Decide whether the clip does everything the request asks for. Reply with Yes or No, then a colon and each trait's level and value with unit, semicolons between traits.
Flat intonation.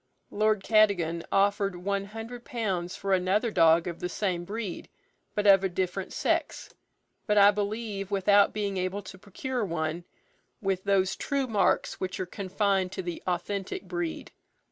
Yes: narrow, 2.3 semitones